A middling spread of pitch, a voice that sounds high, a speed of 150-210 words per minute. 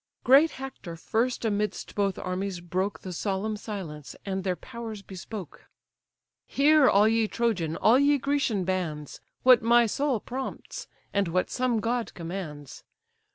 No: average, 4.6 semitones; high, 210 Hz; average, 140 wpm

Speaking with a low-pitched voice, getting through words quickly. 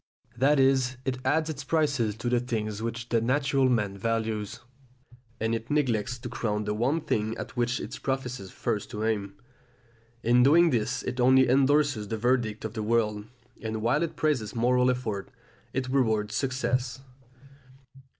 No: low, 120 Hz; average, 160 wpm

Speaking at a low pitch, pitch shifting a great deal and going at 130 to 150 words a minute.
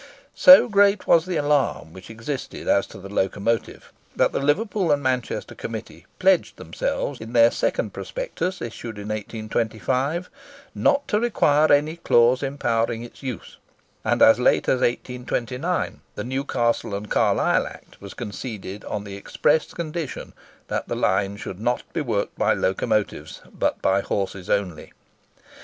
Yes: low, 120 Hz; wide, 6.1 semitones; average, 145 wpm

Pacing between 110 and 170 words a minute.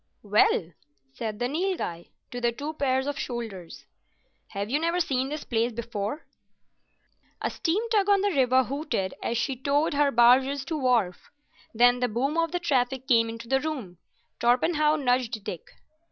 Yes: average, 165 wpm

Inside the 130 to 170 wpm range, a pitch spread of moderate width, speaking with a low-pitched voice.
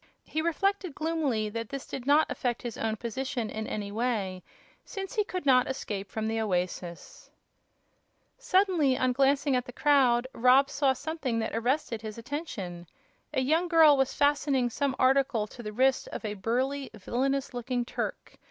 No: average, 165 wpm; average, 4.2 semitones; very high, 255 Hz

